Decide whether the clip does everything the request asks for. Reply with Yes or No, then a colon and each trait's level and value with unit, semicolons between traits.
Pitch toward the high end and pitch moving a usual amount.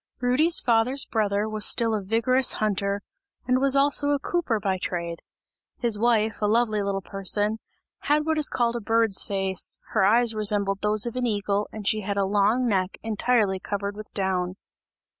Yes: high, 215 Hz; average, 3.2 semitones